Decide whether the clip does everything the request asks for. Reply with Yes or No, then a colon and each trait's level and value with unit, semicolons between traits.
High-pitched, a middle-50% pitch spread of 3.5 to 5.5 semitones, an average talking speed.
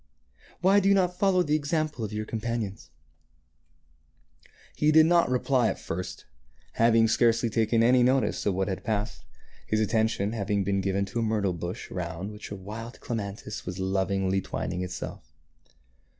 No: low, 110 Hz; average, 4.2 semitones; average, 165 wpm